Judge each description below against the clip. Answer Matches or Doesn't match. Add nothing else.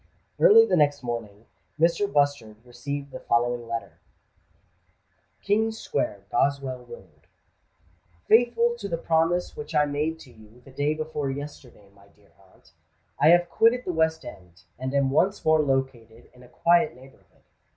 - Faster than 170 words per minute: Doesn't match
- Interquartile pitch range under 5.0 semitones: Doesn't match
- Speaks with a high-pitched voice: Doesn't match